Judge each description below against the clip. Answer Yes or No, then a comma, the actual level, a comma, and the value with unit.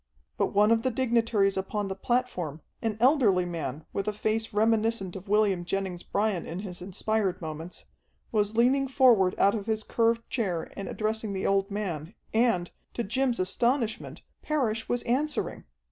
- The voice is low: No, high, 210 Hz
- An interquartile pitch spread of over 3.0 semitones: Yes, average, 3.4 semitones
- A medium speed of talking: Yes, average, 160 wpm